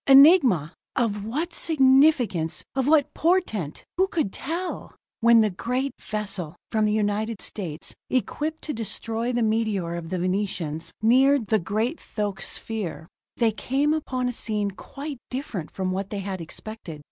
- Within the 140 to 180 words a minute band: Yes, average, 150 wpm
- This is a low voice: No, high, 220 Hz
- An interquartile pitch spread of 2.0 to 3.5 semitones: No, wide, 5.6 semitones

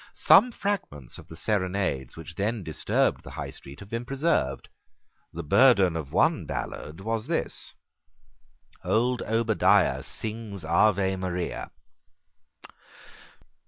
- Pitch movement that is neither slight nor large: No, wide, 5.7 semitones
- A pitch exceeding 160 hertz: No, low, 100 Hz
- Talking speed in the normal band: No, slow, 115 wpm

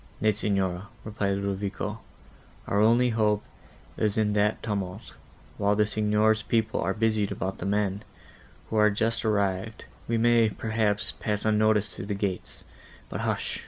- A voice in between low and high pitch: No, low, 105 Hz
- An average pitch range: No, narrow, 1.6 semitones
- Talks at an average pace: Yes, average, 150 wpm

